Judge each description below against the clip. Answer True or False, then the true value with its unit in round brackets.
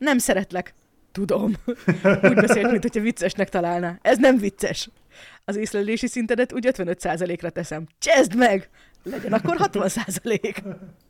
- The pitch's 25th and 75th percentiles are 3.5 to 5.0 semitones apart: True (4.6 semitones)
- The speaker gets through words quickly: False (120 wpm)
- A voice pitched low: False (200 Hz)